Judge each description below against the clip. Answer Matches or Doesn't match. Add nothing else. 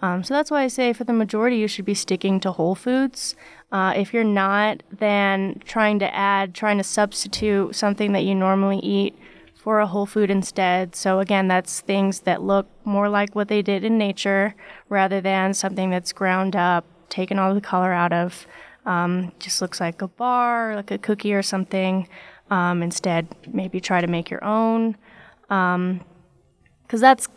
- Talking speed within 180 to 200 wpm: Matches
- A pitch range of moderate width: Doesn't match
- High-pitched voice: Matches